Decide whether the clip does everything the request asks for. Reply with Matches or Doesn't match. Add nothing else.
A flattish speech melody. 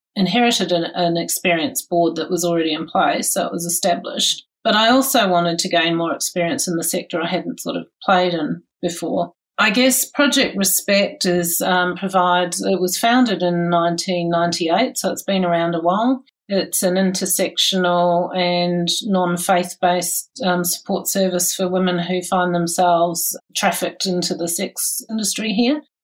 Matches